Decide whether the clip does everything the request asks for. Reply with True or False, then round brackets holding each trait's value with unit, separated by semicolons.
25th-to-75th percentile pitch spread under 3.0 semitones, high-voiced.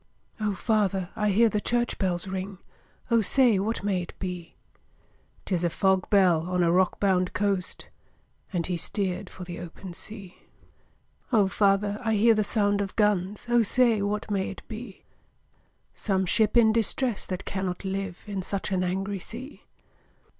True (2.6 semitones; 195 Hz)